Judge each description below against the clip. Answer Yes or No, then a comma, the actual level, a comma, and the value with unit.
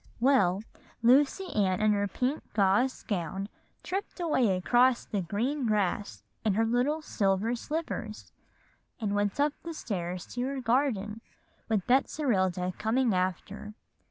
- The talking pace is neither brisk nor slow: No, slow, 130 wpm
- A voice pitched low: No, high, 220 Hz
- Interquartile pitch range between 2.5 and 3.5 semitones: No, average, 5.1 semitones